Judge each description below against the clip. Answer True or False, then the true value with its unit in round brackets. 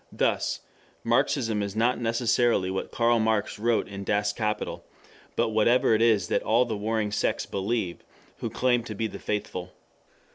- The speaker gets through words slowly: False (160 wpm)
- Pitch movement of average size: False (2.3 semitones)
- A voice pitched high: False (110 Hz)